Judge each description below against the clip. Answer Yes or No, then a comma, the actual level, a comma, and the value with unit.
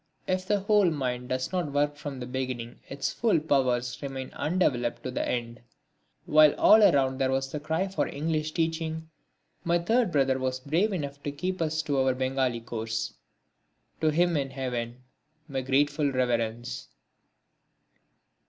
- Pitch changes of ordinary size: Yes, average, 4.0 semitones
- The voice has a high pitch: No, medium, 140 Hz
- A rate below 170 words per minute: Yes, average, 155 wpm